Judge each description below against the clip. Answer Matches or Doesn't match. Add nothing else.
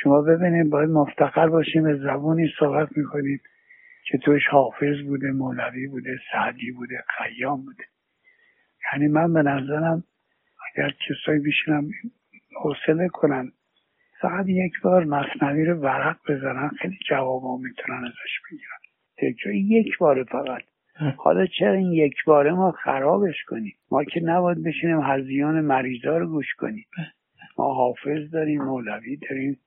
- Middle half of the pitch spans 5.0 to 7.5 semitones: Doesn't match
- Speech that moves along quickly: Doesn't match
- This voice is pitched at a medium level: Matches